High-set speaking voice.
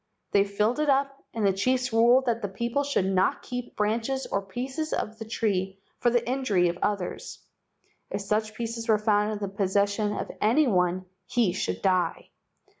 Yes: high, 215 Hz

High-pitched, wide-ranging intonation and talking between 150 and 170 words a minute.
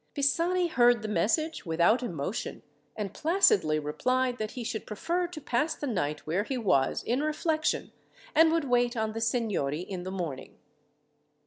Yes: high, 235 Hz; wide, 8.2 semitones; average, 160 wpm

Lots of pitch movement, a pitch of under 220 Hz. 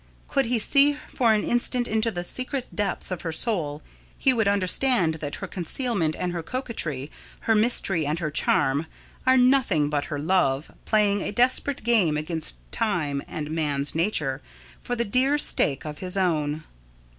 Yes: wide, 7.6 semitones; medium, 185 Hz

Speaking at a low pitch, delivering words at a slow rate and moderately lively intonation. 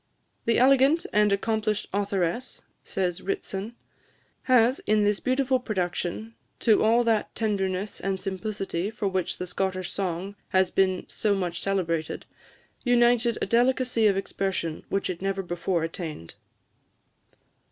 No: high, 200 Hz; slow, 130 wpm; average, 3.5 semitones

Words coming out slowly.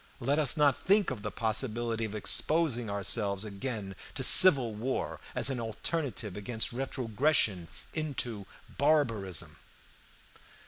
Yes: slow, 120 wpm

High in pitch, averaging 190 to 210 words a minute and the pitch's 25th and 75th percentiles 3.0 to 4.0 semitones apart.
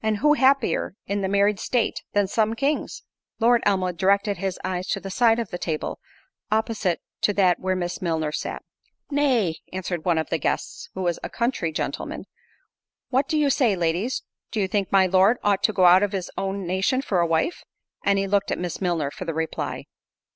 Yes: high, 195 Hz; average, 200 wpm; average, 3.7 semitones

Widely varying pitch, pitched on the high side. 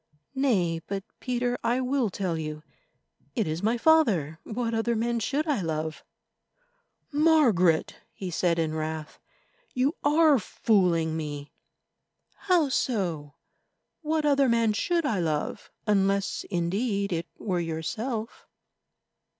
Yes: wide, 7.4 semitones; high, 210 Hz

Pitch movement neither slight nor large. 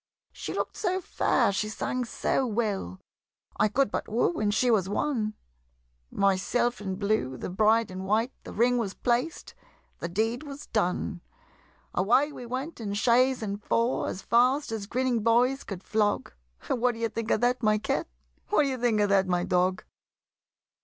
Yes: average, 3.6 semitones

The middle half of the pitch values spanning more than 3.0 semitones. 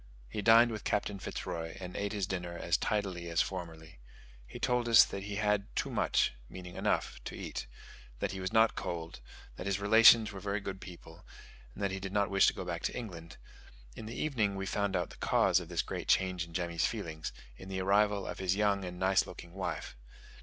No: average, 2.7 semitones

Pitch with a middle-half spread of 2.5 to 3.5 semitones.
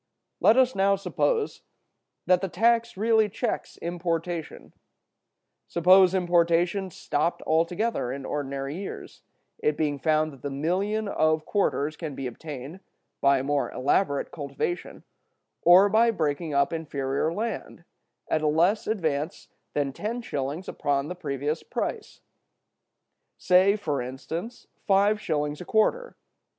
No: wide, 5.4 semitones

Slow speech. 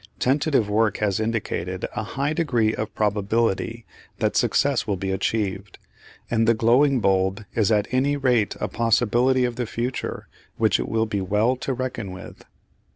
No: average, 160 wpm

